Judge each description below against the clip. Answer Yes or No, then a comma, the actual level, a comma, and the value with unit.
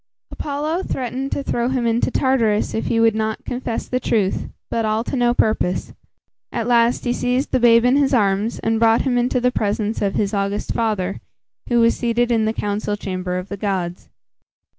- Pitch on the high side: Yes, high, 230 Hz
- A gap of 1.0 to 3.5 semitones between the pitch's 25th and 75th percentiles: Yes, average, 3.0 semitones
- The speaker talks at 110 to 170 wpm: No, average, 195 wpm